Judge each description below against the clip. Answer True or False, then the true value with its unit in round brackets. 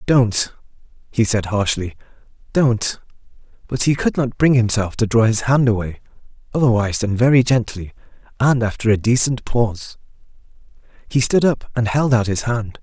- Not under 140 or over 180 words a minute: True (155 wpm)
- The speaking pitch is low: True (115 Hz)